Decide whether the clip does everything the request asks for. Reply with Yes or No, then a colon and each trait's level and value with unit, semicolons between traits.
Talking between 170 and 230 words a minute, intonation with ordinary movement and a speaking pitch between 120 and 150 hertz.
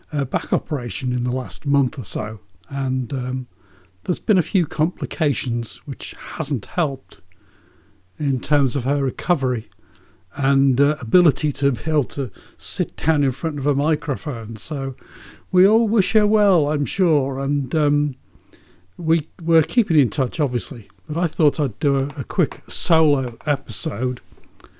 No: average, 150 wpm; average, 4.1 semitones; medium, 140 Hz